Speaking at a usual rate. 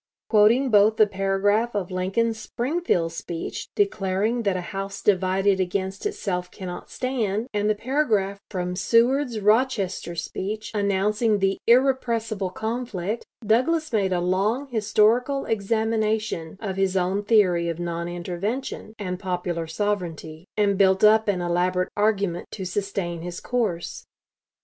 No: slow, 130 wpm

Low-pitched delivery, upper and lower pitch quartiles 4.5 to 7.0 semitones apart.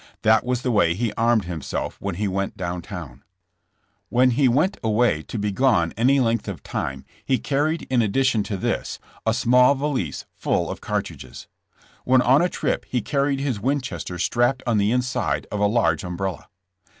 Yes: low, 115 Hz; average, 4.9 semitones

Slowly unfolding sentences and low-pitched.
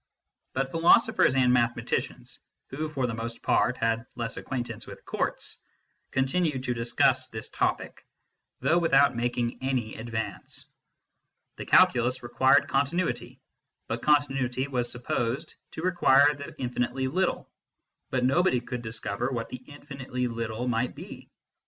Yes: slow, 130 wpm; low, 125 Hz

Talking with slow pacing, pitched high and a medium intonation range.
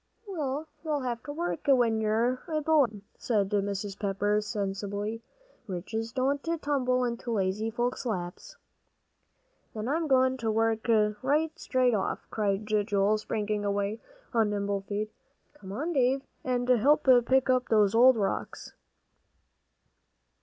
Yes: slow, 130 wpm; high, 225 Hz; average, 4.0 semitones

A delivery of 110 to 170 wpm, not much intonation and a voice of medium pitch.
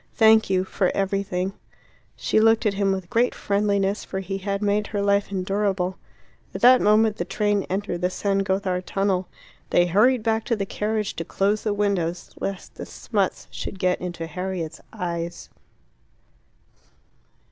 No: average, 160 wpm; narrow, 2.1 semitones; high, 195 Hz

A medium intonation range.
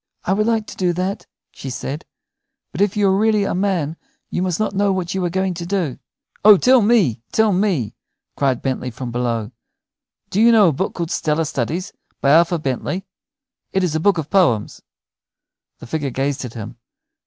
No: wide, 6.4 semitones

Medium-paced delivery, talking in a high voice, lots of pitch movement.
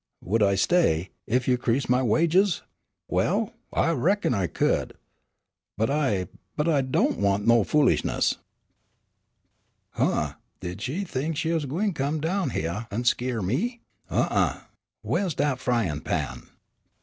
No: average, 150 wpm; low, 130 Hz; wide, 7.1 semitones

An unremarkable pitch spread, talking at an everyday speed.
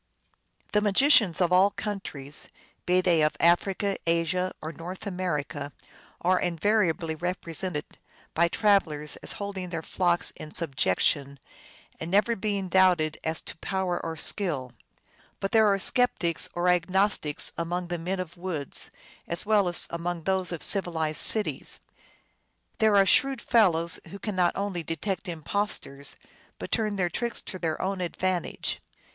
Yes: average, 3.2 semitones; average, 145 wpm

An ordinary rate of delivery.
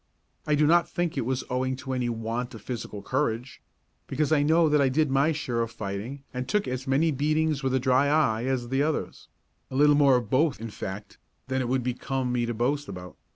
No: fast, 225 wpm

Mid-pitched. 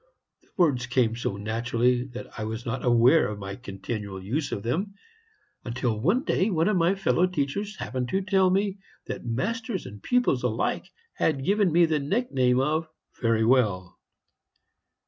No: low, 130 Hz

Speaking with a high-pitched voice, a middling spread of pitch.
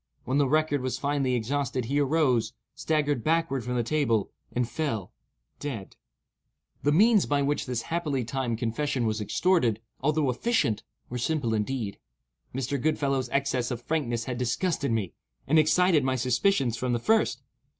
No: low, 135 Hz; average, 4.2 semitones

